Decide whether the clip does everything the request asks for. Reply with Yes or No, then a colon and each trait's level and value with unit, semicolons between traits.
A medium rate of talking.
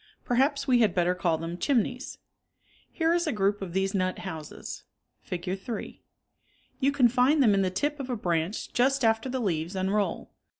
Yes: average, 180 wpm